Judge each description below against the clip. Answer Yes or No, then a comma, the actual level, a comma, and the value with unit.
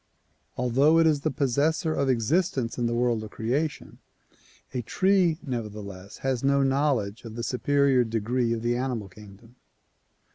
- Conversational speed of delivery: Yes, average, 150 wpm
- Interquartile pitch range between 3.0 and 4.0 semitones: Yes, average, 3.7 semitones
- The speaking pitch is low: Yes, low, 125 Hz